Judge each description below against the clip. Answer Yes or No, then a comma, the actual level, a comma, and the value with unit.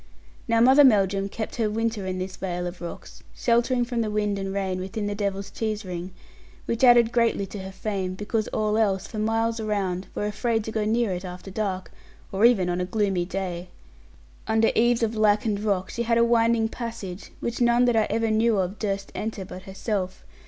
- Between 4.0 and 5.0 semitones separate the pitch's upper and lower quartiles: No, average, 3.0 semitones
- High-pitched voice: Yes, high, 210 Hz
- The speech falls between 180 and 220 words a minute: Yes, average, 200 wpm